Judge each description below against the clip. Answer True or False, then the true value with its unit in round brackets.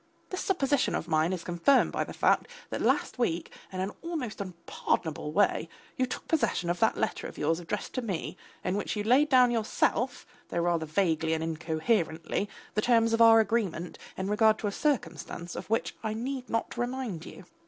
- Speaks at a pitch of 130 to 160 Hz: False (210 Hz)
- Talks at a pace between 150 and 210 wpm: True (190 wpm)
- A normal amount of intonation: False (6.0 semitones)